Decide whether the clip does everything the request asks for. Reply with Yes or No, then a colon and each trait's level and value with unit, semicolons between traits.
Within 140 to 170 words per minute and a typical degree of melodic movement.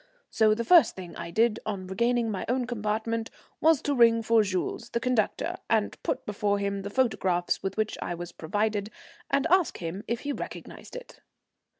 No: average, 185 wpm; average, 3.1 semitones